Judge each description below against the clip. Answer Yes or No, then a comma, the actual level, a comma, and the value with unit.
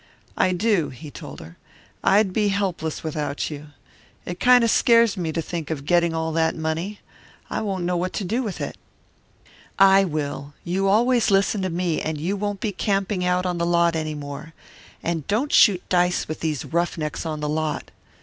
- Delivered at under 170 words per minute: No, average, 190 wpm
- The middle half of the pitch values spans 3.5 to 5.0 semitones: Yes, average, 3.8 semitones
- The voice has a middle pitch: Yes, medium, 175 Hz